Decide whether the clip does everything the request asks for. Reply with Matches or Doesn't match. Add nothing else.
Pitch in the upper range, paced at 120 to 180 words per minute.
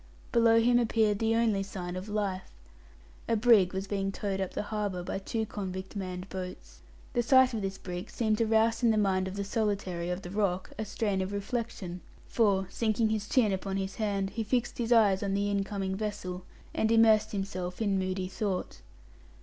Doesn't match